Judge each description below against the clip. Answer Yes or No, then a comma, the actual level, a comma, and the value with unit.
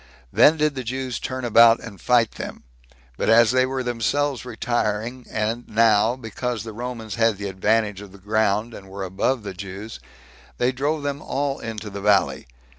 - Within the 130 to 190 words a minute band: Yes, average, 180 wpm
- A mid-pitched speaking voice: No, low, 115 Hz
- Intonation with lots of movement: No, average, 3.4 semitones